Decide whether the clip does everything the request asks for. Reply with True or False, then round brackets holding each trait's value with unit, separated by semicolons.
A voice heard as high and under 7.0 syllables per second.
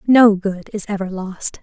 True (200 Hz; 4.1 syllables/s)